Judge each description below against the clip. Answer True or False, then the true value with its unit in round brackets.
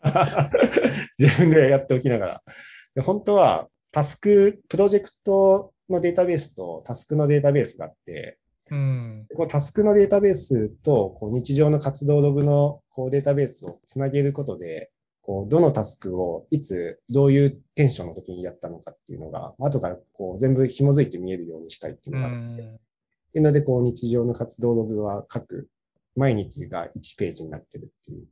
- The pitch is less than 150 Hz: True (140 Hz)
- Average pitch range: True (4.3 semitones)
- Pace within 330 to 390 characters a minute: True (360 characters per minute)